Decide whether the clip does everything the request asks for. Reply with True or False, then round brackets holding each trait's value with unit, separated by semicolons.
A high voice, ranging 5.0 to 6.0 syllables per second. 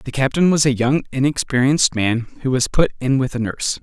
False (135 Hz; 5.5 syllables/s)